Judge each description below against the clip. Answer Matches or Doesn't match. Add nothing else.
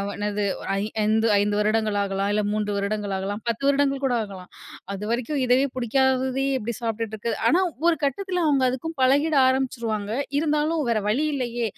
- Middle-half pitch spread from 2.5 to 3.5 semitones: Doesn't match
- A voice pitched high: Matches